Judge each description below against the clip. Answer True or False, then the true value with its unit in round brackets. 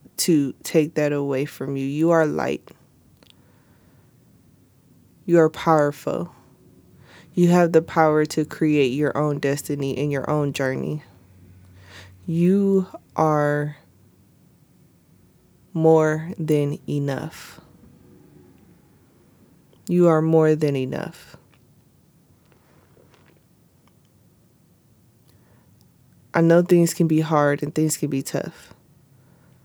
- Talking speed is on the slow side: True (95 wpm)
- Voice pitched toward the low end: False (150 Hz)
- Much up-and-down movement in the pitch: False (2.5 semitones)